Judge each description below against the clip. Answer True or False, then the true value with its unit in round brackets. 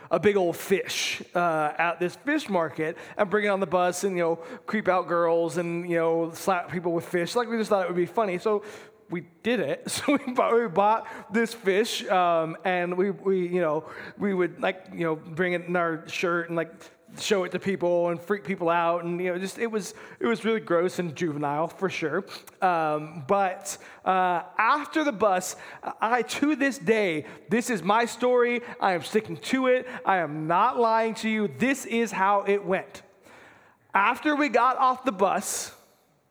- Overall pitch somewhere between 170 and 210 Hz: True (190 Hz)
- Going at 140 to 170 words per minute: False (205 wpm)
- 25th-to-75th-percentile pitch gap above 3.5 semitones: True (4.6 semitones)